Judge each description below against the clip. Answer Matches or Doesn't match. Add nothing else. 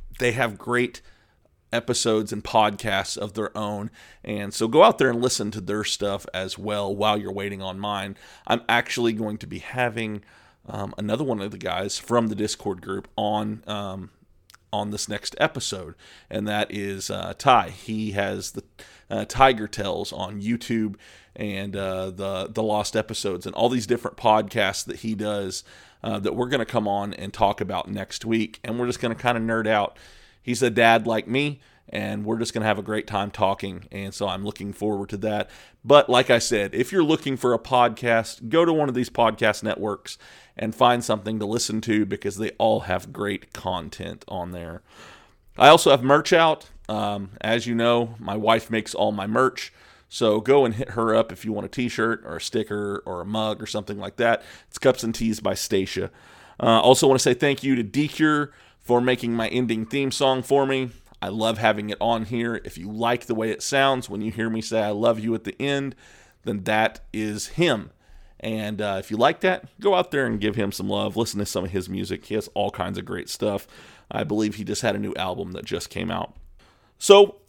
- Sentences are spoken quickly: Matches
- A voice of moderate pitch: Doesn't match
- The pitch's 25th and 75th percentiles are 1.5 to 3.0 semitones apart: Matches